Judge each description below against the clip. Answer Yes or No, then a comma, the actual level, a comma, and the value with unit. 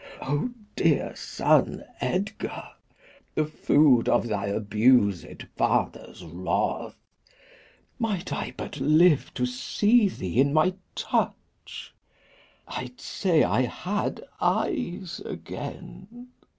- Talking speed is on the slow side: Yes, slow, 100 wpm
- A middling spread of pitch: No, wide, 7.6 semitones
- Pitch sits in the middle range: Yes, medium, 145 Hz